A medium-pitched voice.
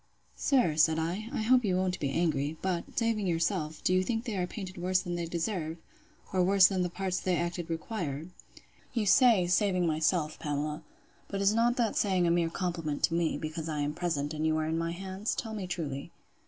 Yes: medium, 175 Hz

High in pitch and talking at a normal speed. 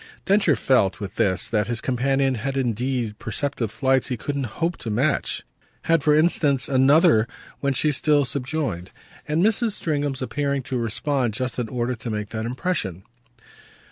No: low, 130 Hz; average, 160 wpm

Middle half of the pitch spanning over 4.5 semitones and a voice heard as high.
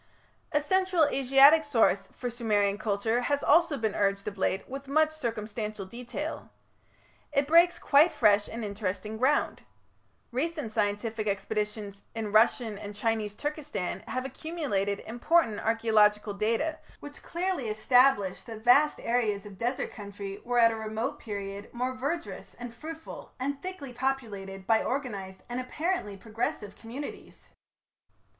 Yes: average, 5.1 semitones; high, 230 Hz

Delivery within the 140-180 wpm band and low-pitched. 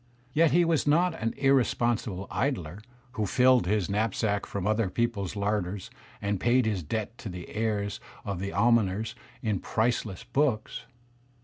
Yes: average, 145 wpm; low, 110 Hz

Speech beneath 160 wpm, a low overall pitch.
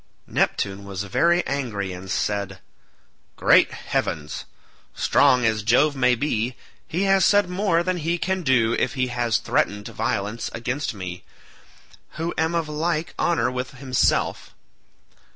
Yes: slow, 135 wpm; low, 125 Hz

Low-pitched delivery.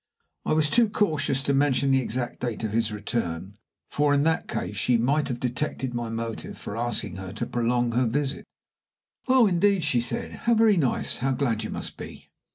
Yes: low, 125 Hz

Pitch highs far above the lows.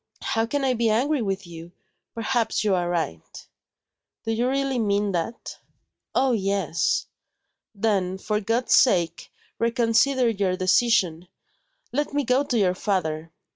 No: average, 4.8 semitones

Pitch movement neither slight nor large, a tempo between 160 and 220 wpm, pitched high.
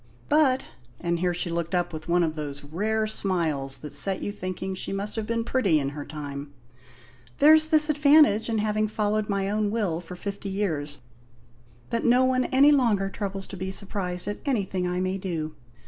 Yes: average, 4.3 semitones; average, 190 wpm; high, 195 Hz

